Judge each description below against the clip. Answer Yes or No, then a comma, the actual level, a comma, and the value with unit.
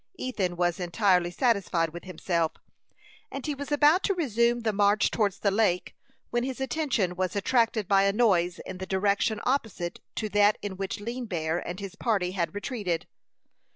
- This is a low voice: No, high, 200 Hz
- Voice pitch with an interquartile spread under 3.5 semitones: No, average, 4.7 semitones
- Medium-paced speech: Yes, average, 175 wpm